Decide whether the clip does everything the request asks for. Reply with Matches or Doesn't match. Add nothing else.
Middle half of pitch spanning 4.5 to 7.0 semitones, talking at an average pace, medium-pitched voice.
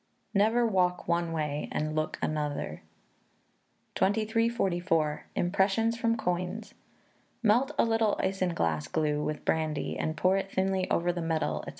Doesn't match